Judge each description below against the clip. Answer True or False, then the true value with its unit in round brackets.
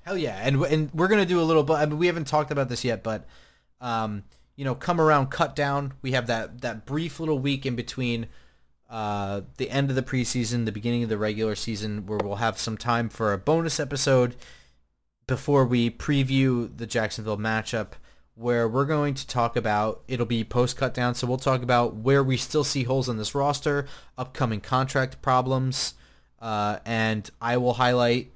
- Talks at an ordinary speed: True (195 wpm)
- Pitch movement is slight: False (3.7 semitones)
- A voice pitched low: True (125 Hz)